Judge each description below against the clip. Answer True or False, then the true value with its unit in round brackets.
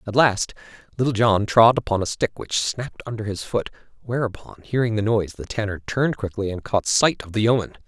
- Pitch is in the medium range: False (110 Hz)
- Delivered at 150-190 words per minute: False (205 wpm)